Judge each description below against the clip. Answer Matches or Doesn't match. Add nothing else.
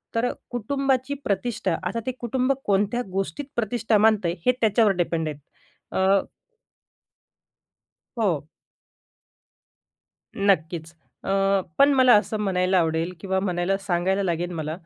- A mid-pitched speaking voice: Doesn't match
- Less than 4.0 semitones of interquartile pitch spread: Doesn't match